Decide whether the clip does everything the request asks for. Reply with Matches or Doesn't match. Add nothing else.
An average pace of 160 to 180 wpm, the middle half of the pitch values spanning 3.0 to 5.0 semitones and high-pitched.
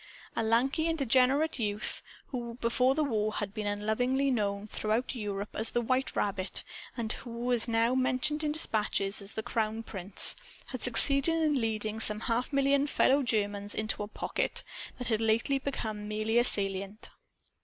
Matches